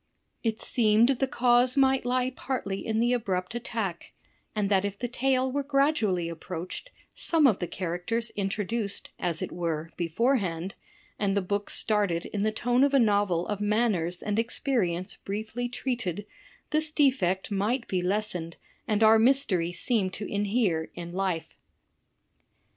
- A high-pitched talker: Yes, high, 210 Hz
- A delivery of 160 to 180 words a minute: No, average, 150 wpm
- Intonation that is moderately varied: Yes, average, 5.0 semitones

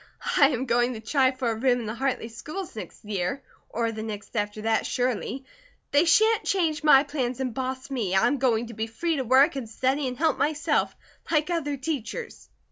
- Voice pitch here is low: No, very high, 260 Hz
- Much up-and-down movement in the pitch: No, average, 4.2 semitones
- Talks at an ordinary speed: No, fast, 210 wpm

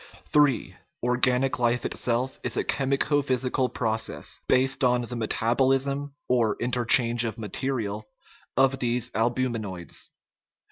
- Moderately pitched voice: No, low, 125 Hz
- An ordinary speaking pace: No, slow, 125 wpm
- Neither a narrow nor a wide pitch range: No, narrow, 2.2 semitones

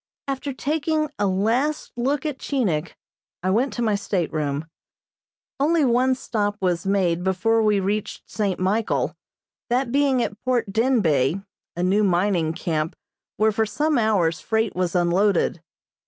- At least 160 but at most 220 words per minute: No, average, 140 wpm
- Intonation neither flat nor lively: No, wide, 5.8 semitones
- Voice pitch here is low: No, high, 210 Hz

